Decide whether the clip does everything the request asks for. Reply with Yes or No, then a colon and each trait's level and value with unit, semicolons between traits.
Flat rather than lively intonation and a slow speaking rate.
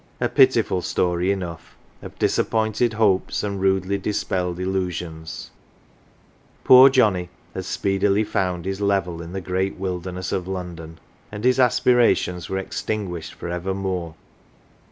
Yes: narrow, 2.1 semitones; slow, 125 wpm